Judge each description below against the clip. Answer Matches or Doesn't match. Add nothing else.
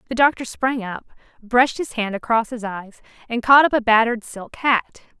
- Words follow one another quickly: Doesn't match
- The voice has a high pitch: Matches